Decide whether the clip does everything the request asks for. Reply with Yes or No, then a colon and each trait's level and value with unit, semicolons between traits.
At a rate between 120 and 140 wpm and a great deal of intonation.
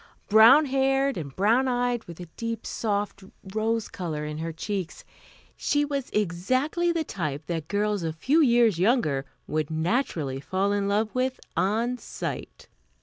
No: average, 150 wpm; wide, 7.0 semitones